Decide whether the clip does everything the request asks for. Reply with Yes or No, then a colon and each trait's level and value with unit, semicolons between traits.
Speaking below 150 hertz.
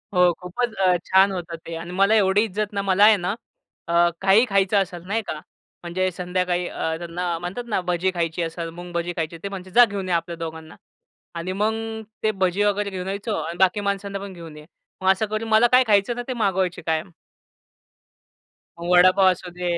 No: medium, 185 Hz